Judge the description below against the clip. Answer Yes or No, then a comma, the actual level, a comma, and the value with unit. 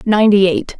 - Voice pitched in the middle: No, high, 200 Hz